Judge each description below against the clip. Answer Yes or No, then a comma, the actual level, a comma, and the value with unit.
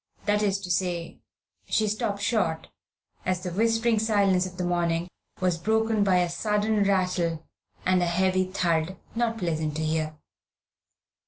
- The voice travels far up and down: No, average, 3.4 semitones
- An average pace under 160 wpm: Yes, average, 150 wpm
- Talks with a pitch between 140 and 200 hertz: Yes, medium, 185 Hz